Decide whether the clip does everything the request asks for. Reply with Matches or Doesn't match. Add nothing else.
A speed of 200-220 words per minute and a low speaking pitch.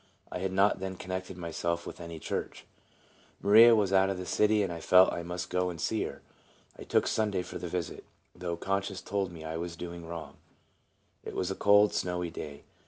Matches